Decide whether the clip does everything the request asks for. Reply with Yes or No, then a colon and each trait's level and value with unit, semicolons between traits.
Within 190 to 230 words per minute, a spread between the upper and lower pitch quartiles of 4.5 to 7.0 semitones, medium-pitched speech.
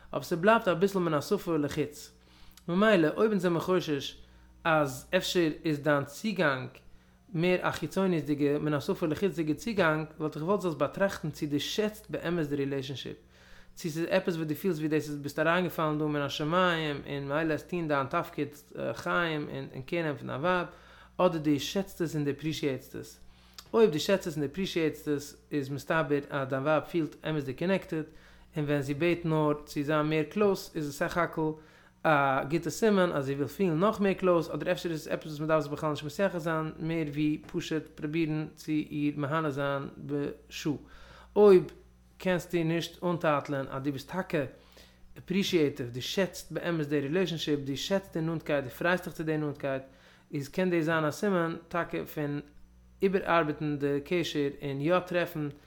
No: average, 195 wpm; average, 3.2 semitones; medium, 155 Hz